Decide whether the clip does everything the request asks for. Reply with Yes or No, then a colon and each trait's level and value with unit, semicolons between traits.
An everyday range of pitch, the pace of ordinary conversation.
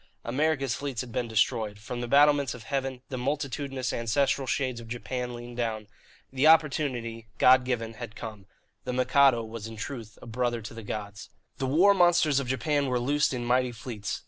Yes: average, 3.1 semitones; average, 185 wpm